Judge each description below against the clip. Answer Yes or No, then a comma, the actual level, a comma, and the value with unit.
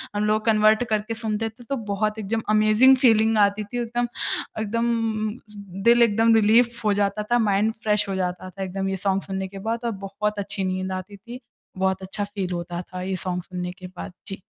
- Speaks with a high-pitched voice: Yes, high, 210 Hz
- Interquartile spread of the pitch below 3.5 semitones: Yes, narrow, 2.6 semitones